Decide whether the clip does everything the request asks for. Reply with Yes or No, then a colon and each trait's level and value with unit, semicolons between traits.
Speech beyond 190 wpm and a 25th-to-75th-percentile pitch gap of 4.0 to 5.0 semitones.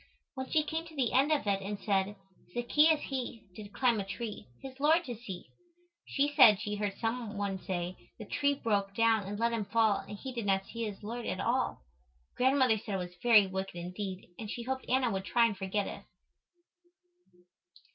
Yes: average, 200 wpm; average, 4.3 semitones